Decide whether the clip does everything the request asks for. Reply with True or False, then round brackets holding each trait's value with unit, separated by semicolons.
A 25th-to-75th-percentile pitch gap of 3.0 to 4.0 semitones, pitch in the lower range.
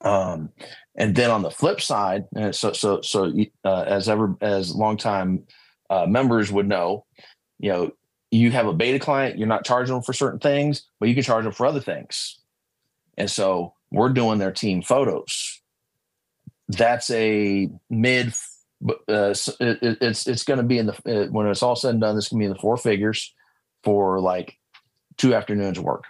True (3.5 semitones; 110 Hz)